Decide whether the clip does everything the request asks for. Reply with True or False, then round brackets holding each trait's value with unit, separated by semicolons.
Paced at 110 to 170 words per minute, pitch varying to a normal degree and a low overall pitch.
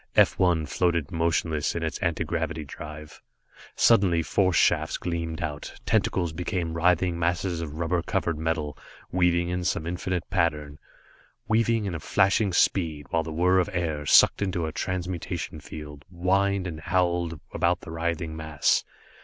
False (150 wpm; 2.2 semitones; 85 Hz)